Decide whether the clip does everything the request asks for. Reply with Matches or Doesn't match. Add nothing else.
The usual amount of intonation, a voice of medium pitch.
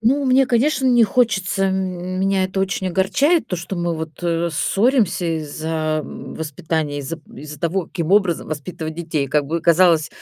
Matches